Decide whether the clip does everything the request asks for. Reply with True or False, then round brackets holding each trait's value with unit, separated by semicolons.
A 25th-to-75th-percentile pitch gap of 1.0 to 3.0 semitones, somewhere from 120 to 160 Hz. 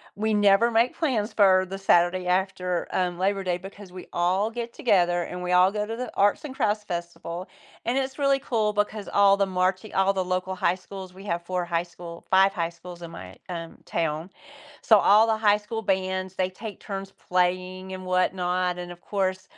False (2.4 semitones; 185 Hz)